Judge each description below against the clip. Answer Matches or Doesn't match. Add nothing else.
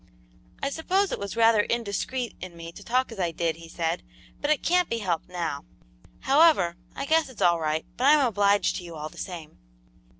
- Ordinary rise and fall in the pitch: Doesn't match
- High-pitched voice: Matches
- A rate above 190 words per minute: Matches